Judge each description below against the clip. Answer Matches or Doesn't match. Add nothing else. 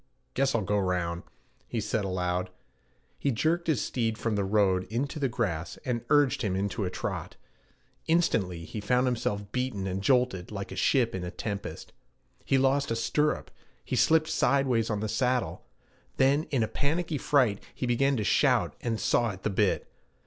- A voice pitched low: Matches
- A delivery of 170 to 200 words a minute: Matches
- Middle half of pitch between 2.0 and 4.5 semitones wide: Doesn't match